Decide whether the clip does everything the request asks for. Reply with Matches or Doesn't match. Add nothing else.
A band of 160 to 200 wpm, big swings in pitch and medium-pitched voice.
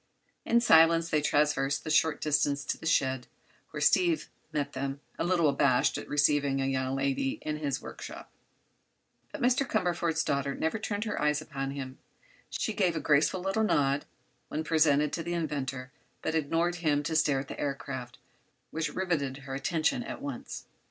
Doesn't match